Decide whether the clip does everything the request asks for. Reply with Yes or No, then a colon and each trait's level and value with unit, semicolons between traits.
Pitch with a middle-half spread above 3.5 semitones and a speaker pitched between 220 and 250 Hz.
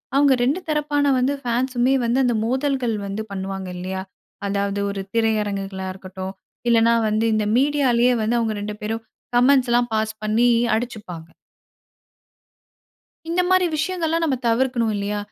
Yes: average, 4.2 semitones; high, 230 Hz